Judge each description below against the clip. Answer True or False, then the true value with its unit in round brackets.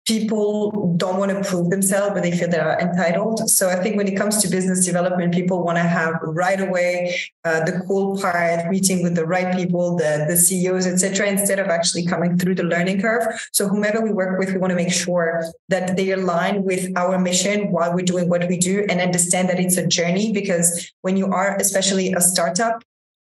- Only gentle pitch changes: True (1.9 semitones)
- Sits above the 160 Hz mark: True (185 Hz)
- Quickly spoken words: True (215 wpm)